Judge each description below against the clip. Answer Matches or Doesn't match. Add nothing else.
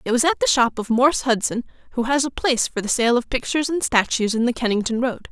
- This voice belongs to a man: Doesn't match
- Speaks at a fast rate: Matches